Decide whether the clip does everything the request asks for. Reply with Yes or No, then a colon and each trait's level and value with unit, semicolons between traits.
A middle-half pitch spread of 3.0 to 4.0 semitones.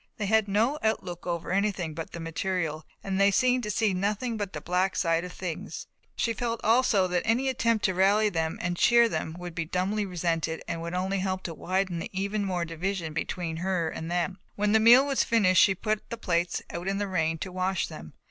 Yes: average, 3.6 semitones